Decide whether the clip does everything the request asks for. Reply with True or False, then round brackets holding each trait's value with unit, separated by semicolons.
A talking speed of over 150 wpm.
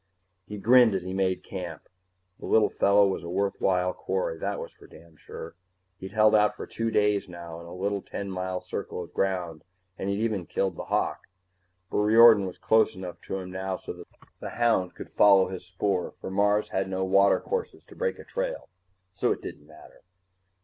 True (200 wpm)